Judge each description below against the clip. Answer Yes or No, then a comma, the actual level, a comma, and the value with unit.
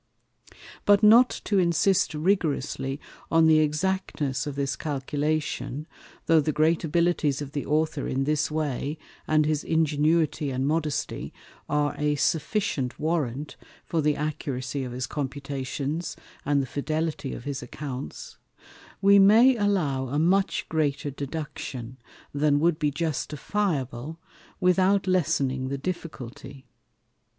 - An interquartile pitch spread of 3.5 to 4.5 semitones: No, average, 3.0 semitones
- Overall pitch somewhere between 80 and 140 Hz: No, medium, 150 Hz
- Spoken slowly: Yes, slow, 125 wpm